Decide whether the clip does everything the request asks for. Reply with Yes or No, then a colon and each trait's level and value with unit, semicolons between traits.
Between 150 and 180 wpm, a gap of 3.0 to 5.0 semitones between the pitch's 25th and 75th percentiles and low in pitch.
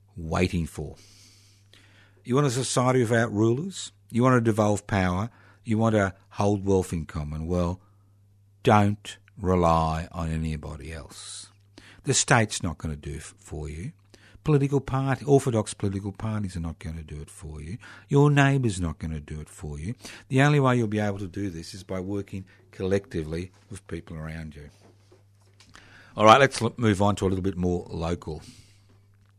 Yes: average, 175 wpm; average, 3.7 semitones; low, 100 Hz